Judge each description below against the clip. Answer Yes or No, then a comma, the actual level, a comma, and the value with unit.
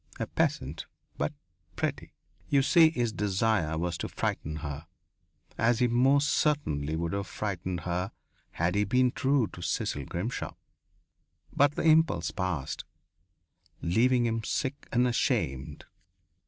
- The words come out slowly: Yes, slow, 130 wpm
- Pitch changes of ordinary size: No, wide, 7.1 semitones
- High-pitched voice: No, low, 105 Hz